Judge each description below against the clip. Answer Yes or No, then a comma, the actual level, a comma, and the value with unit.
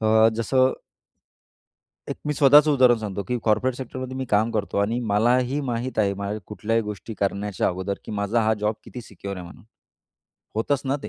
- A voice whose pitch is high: No, low, 110 Hz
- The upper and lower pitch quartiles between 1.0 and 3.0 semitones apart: No, average, 3.9 semitones